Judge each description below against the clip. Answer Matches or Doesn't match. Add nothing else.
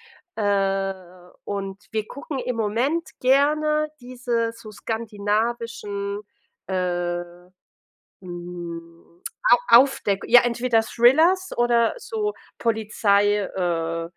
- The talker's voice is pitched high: Matches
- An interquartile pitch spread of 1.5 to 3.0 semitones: Doesn't match